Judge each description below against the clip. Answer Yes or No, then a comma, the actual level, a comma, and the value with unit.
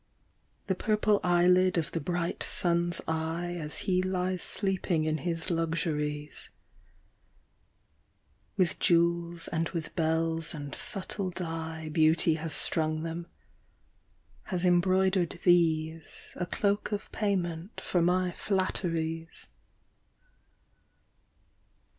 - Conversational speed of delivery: No, slow, 100 wpm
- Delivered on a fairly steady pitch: Yes, narrow, 2.2 semitones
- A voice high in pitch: No, medium, 170 Hz